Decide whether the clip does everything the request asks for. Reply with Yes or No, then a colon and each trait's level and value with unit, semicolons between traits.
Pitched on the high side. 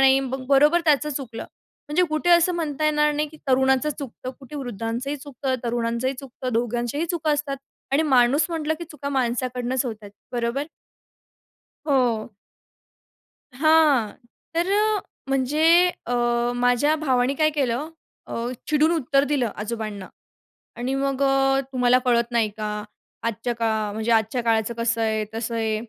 Yes: very high, 260 Hz